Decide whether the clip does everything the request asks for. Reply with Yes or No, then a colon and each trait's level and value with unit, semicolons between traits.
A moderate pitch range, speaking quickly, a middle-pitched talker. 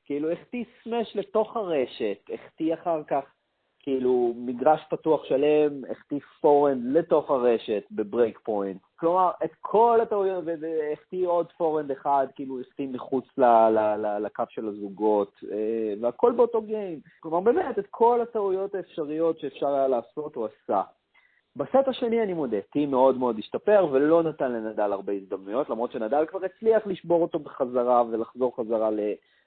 No: wide, 7.4 semitones; fast, 155 wpm; medium, 150 Hz